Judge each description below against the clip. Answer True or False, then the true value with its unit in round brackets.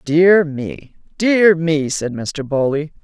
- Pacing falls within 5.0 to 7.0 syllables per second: False (3.0 syllables/s)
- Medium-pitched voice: True (160 Hz)